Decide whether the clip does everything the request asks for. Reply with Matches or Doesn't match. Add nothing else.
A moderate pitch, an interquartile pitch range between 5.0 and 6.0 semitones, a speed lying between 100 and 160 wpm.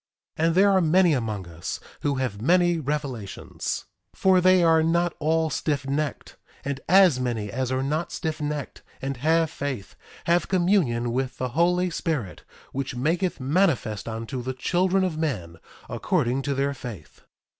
Matches